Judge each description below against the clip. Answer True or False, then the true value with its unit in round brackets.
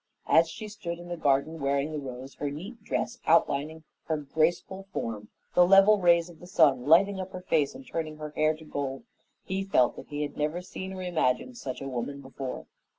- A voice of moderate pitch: True (160 Hz)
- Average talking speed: False (210 wpm)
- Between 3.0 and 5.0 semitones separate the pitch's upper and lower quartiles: True (4.4 semitones)